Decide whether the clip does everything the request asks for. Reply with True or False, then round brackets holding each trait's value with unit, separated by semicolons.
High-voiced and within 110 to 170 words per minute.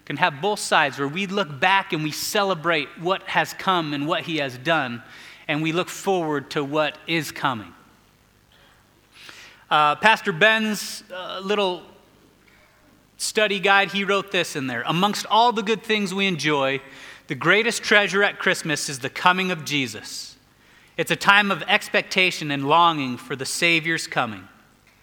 False (175 Hz; 160 wpm)